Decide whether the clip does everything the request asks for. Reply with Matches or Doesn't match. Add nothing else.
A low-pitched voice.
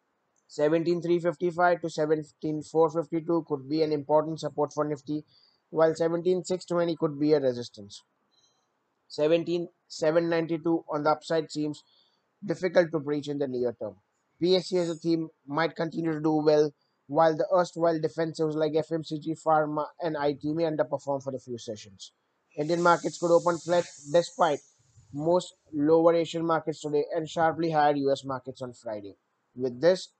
Doesn't match